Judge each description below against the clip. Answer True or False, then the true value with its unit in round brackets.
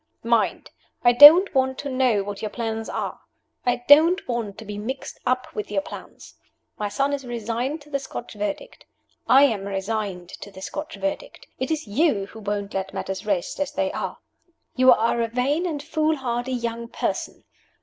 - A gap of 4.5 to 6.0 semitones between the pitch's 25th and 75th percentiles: True (5.3 semitones)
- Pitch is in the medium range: False (240 Hz)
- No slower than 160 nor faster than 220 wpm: True (180 wpm)